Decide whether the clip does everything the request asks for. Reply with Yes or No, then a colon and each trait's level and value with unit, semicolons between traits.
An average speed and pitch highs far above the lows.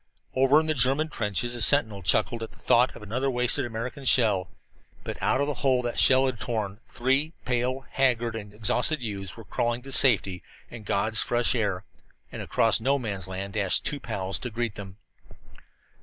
No: average, 190 wpm; average, 3.9 semitones